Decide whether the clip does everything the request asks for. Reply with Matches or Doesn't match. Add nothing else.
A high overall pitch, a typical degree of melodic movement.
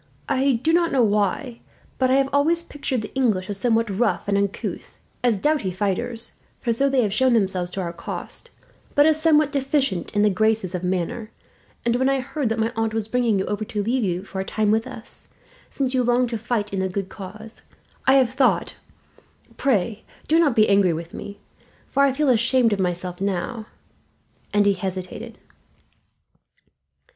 Matches